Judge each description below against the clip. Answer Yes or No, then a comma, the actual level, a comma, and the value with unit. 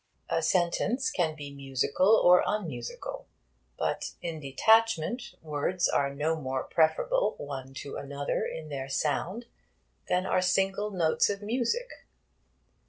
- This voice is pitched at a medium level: Yes, medium, 165 Hz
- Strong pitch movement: Yes, wide, 6.5 semitones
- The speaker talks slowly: Yes, slow, 125 wpm